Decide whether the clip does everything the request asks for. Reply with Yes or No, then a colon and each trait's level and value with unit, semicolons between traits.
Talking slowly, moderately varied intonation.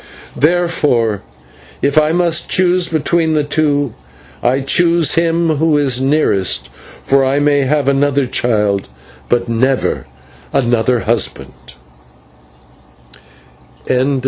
Yes: slow, 100 wpm; average, 4.5 semitones